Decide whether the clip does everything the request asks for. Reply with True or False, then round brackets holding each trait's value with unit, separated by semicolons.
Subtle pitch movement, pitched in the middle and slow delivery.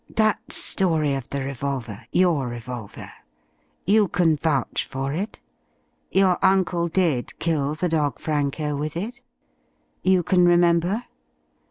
False (4.6 semitones; 160 Hz; 125 wpm)